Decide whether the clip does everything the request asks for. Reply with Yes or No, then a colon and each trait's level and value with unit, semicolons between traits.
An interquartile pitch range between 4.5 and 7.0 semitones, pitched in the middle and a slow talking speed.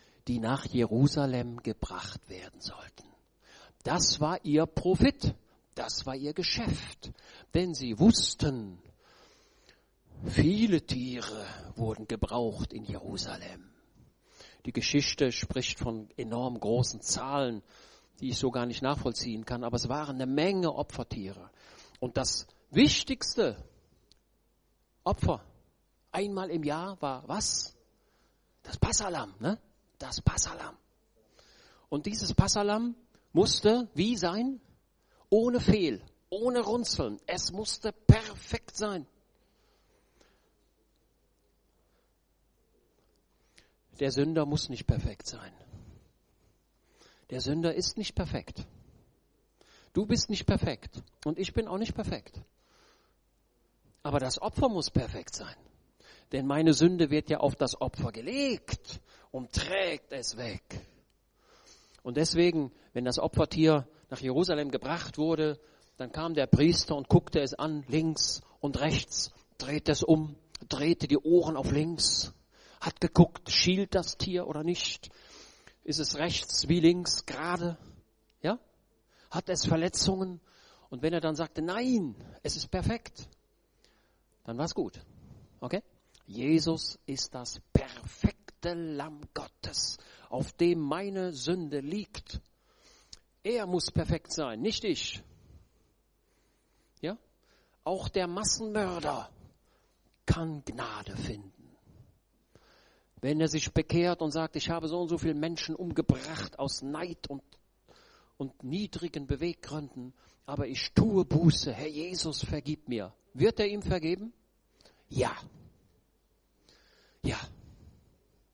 Yes: average, 5.0 semitones; medium, 155 Hz; slow, 115 wpm